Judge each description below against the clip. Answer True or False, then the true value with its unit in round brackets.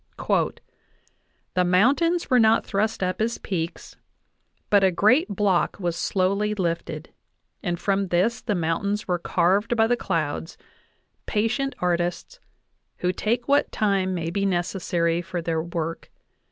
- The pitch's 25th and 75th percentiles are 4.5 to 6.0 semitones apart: False (3.9 semitones)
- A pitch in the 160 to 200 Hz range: True (190 Hz)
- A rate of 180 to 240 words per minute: False (135 wpm)